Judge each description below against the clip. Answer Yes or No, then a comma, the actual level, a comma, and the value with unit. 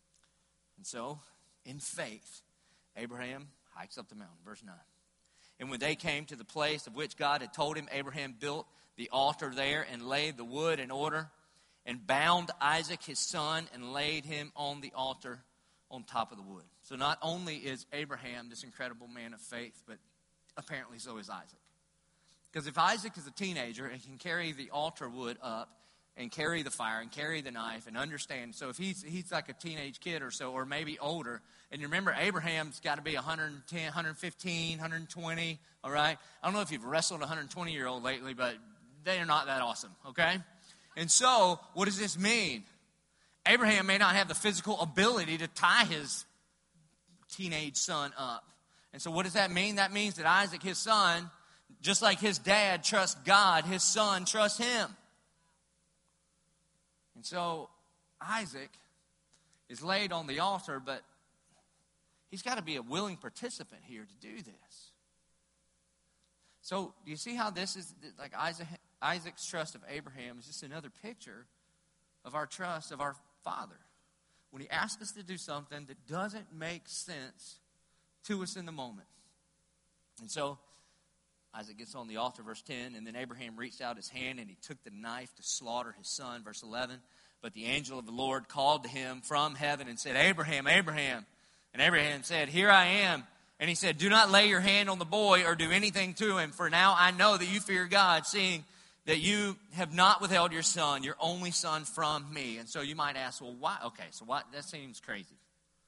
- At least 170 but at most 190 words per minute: Yes, average, 185 wpm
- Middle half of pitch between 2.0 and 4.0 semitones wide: No, average, 4.8 semitones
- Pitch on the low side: No, medium, 165 Hz